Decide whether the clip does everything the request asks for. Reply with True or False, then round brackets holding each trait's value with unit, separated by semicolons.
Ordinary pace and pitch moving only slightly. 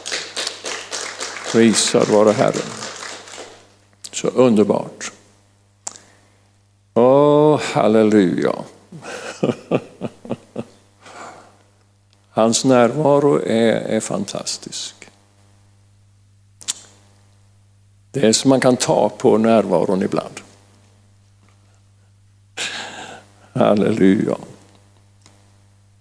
False (55 wpm; 1.7 semitones)